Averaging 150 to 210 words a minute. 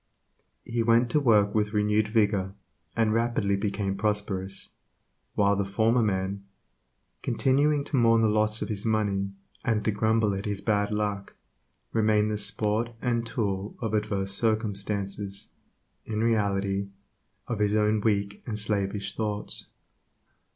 No: slow, 135 wpm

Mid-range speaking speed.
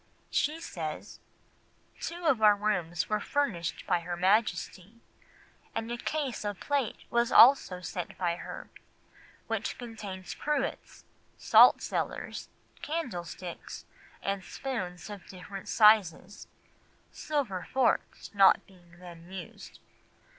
No: slow, 110 wpm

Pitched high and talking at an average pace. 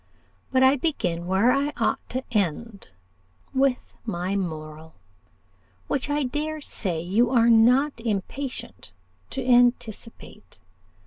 No: high, 235 Hz; slow, 115 wpm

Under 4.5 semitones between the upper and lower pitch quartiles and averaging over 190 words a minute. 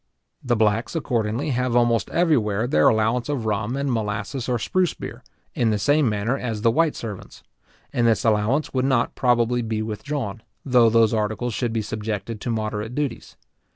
No: average, 2.8 semitones; average, 180 wpm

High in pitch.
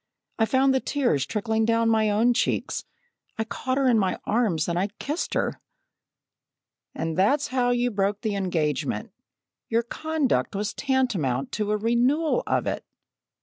Yes: high, 225 Hz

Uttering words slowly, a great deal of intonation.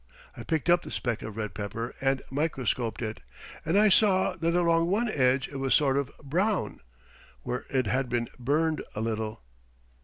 No: average, 180 wpm; wide, 6.1 semitones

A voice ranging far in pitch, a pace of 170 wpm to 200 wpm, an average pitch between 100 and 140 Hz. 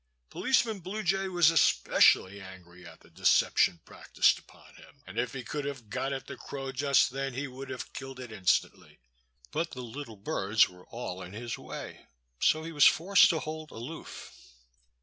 Yes: wide, 6.2 semitones; average, 180 wpm; low, 135 Hz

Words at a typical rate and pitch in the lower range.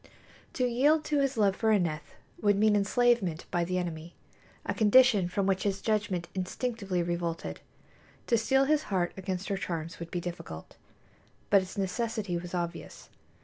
No: average, 160 wpm; high, 195 Hz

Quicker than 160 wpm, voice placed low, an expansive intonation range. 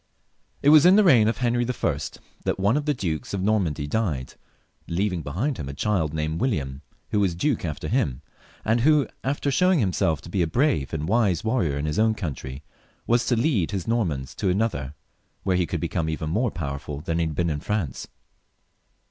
Yes: fast, 205 wpm; very low, 95 Hz; wide, 7.3 semitones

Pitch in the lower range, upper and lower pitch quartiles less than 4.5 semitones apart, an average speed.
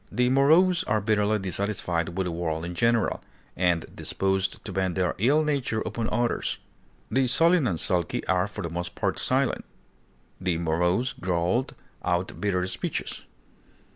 No: very low, 95 Hz; average, 5.2 semitones; average, 150 wpm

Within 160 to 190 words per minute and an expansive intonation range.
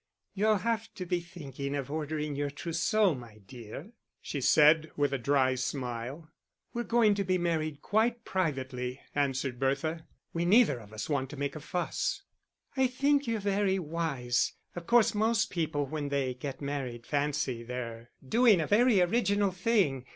Yes: average, 165 wpm; wide, 6.7 semitones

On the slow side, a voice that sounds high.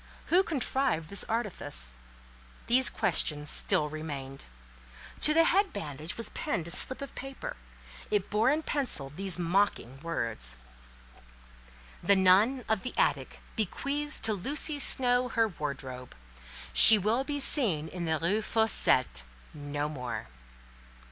Yes: slow, 130 wpm; high, 200 Hz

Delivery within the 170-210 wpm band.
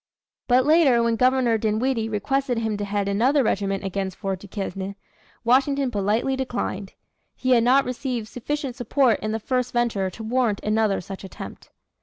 No: average, 160 wpm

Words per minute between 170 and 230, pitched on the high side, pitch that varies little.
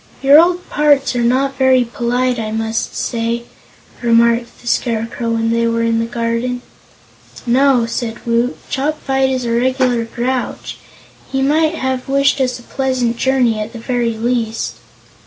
No: average, 155 wpm; high, 245 Hz; narrow, 2.3 semitones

